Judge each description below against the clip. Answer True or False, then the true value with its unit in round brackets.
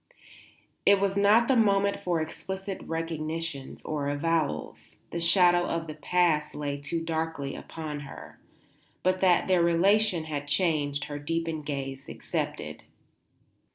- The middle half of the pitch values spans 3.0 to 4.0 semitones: True (3.7 semitones)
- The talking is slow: True (130 wpm)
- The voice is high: False (165 Hz)